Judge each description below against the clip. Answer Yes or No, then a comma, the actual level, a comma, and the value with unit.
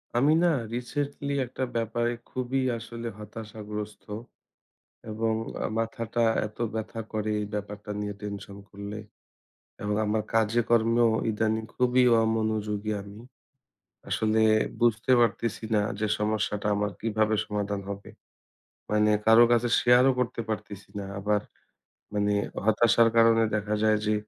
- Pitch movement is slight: Yes, narrow, 1.9 semitones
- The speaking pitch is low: Yes, low, 110 Hz